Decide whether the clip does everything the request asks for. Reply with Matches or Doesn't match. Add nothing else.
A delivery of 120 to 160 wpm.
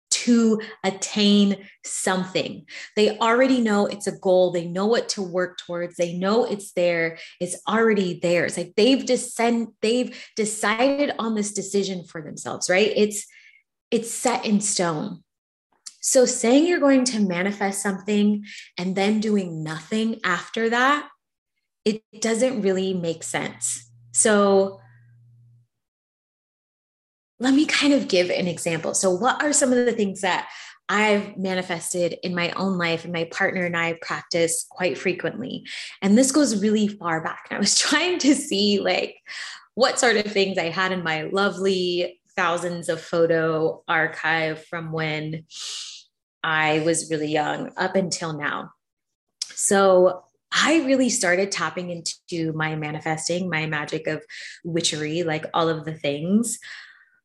Matches